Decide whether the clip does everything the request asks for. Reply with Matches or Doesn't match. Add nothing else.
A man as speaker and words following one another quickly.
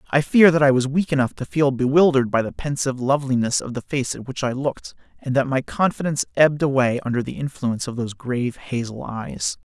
Matches